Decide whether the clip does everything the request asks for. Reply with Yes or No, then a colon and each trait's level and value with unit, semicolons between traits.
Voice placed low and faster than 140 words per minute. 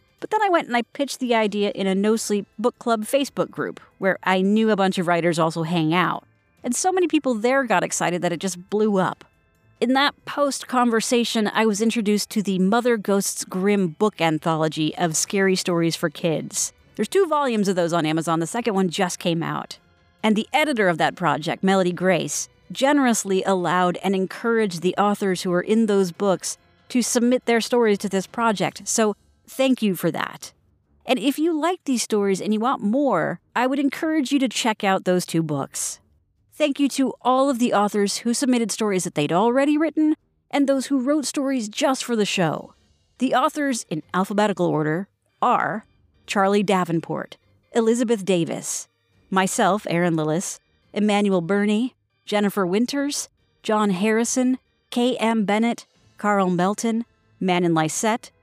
No: high, 210 Hz; average, 175 wpm